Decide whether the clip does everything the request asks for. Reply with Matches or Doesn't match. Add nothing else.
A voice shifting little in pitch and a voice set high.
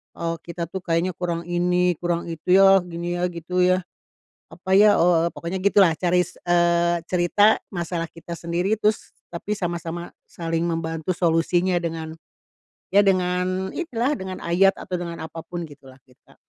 Doesn't match